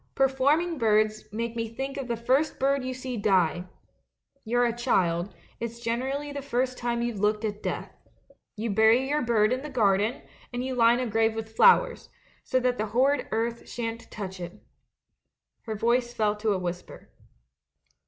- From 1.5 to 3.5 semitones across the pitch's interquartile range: Yes, average, 3.1 semitones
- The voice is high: Yes, high, 235 Hz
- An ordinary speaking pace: Yes, average, 180 wpm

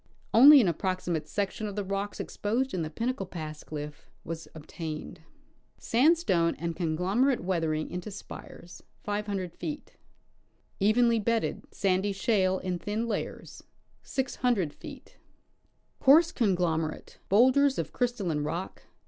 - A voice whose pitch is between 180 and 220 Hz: Yes, high, 190 Hz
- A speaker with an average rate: No, slow, 110 wpm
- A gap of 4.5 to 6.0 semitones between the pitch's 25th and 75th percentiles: Yes, wide, 5.6 semitones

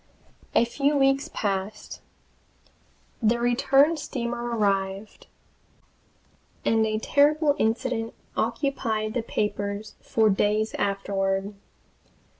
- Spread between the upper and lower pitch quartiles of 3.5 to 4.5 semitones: Yes, average, 4.1 semitones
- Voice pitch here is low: No, high, 225 Hz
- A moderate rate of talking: No, slow, 85 wpm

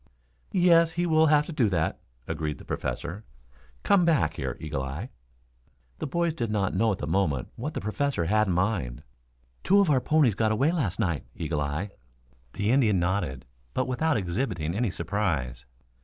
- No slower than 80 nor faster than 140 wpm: No, average, 175 wpm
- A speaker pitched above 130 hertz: No, low, 105 Hz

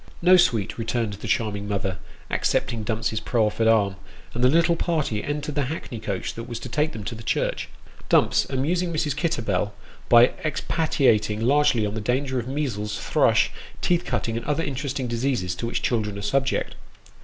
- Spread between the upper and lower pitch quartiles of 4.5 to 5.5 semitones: Yes, average, 5.2 semitones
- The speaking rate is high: No, average, 175 wpm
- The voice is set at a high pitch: No, low, 120 Hz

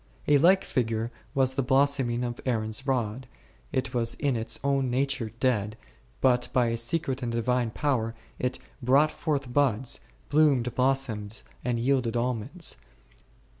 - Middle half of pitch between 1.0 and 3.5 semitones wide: Yes, average, 2.8 semitones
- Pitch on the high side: No, low, 125 Hz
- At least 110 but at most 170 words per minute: Yes, average, 150 wpm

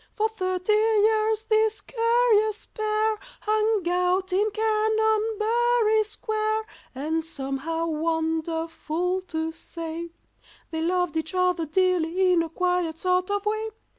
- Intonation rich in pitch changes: No, average, 4.6 semitones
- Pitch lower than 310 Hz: No, very high, 375 Hz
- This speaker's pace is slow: Yes, slow, 115 wpm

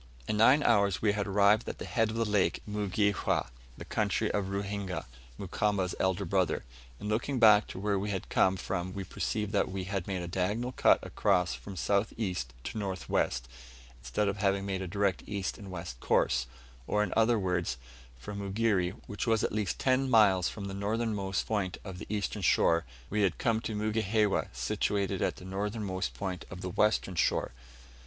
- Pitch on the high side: No, low, 100 Hz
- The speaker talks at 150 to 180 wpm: No, average, 190 wpm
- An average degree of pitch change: No, narrow, 2.2 semitones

